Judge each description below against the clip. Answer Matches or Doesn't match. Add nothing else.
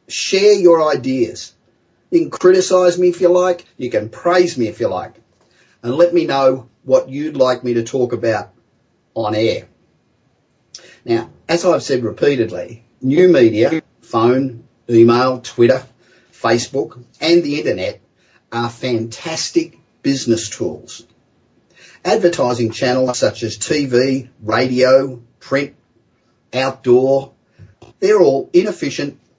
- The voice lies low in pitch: Matches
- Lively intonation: Matches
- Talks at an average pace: Doesn't match